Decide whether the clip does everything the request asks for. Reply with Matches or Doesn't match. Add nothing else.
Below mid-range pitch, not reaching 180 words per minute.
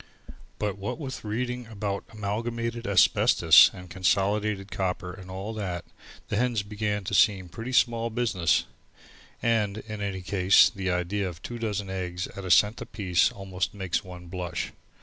Matches